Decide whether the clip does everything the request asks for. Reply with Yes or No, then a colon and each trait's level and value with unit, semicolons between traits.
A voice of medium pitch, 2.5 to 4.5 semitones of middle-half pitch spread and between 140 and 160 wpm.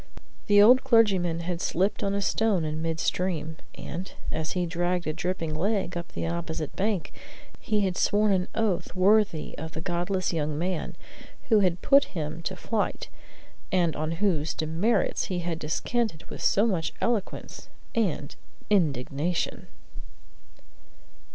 Yes: medium, 180 Hz; average, 3.8 semitones; average, 145 wpm